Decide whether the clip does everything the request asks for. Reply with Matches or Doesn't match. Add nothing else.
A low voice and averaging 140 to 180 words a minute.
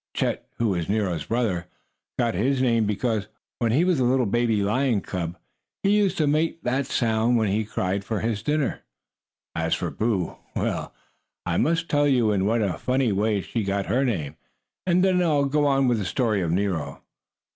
Doesn't match